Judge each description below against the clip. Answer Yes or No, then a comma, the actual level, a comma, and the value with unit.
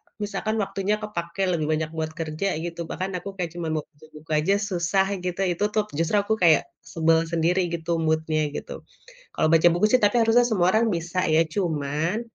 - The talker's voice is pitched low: No, medium, 170 Hz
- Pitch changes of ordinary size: Yes, average, 3.7 semitones